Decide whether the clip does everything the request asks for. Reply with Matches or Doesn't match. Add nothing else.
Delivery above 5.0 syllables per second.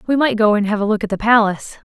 Matches